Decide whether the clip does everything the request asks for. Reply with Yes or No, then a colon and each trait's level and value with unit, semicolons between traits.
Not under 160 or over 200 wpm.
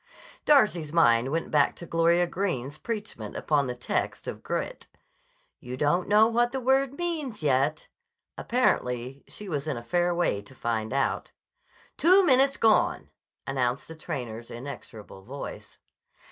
No: average, 145 wpm